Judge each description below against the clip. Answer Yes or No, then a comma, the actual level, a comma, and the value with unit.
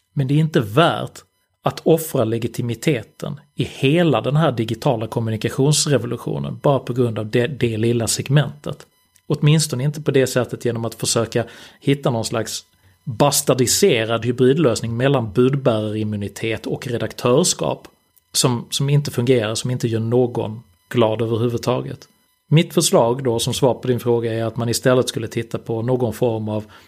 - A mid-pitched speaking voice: No, low, 125 Hz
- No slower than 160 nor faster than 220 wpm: No, average, 150 wpm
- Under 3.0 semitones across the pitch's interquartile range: No, average, 3.5 semitones